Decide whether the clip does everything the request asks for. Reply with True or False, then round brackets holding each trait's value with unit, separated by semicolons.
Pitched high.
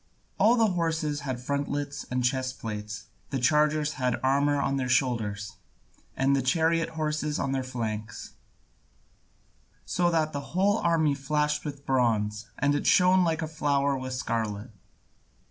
False (140 Hz)